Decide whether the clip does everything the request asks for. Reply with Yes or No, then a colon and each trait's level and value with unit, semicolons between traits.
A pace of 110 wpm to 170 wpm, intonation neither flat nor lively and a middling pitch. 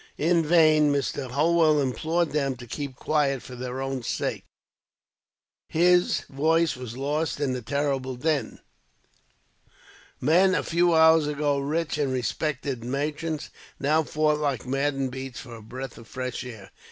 Yes: average, 145 wpm; average, 3.2 semitones; medium, 145 Hz